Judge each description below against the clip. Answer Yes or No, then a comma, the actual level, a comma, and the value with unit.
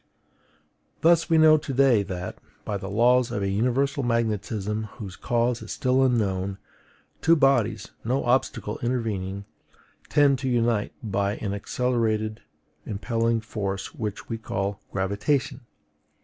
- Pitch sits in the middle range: No, low, 115 Hz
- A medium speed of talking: No, slow, 130 wpm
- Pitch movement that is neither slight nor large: Yes, average, 3.9 semitones